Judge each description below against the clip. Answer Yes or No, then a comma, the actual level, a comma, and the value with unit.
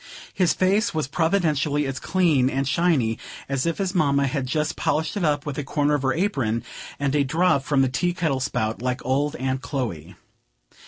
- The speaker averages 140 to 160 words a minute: No, average, 195 wpm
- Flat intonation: No, average, 3.6 semitones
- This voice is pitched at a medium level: Yes, medium, 145 Hz